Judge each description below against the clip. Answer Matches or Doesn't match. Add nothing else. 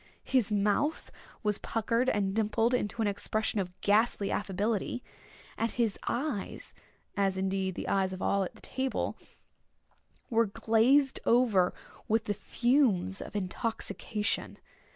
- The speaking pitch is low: Doesn't match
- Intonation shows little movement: Doesn't match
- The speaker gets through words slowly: Matches